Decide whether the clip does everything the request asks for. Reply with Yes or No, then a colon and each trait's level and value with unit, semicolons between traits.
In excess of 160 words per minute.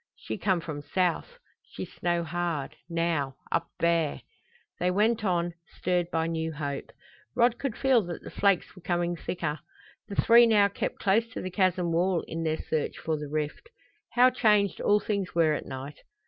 Yes: average, 175 wpm